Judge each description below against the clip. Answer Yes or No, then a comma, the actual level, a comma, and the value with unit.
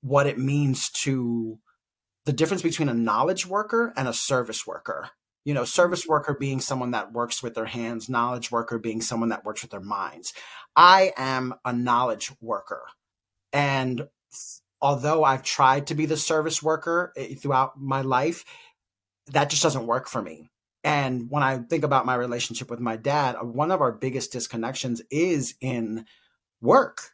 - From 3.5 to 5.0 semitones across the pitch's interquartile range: Yes, average, 4.1 semitones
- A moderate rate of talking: Yes, average, 165 wpm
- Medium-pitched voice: No, low, 130 Hz